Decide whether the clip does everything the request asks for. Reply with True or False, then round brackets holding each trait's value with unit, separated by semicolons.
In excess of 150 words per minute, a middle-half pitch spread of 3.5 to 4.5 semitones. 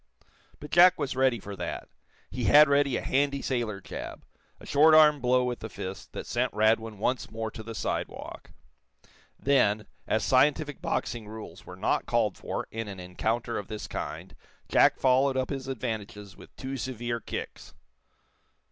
True (165 wpm; 3.8 semitones)